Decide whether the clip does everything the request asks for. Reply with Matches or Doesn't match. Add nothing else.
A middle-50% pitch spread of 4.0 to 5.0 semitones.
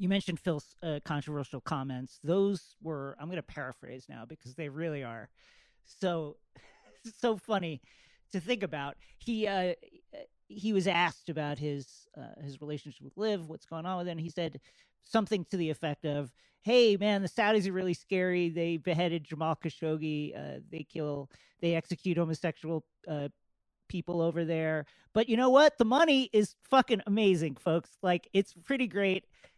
Matches